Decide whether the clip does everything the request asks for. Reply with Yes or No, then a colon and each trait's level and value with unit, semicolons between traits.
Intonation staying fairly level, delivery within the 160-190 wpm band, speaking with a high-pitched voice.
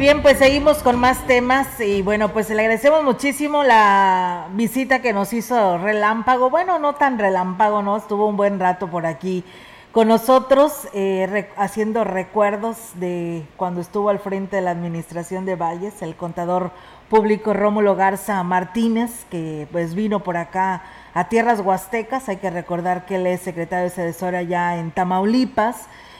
No: average, 4.0 semitones; average, 165 wpm; high, 200 Hz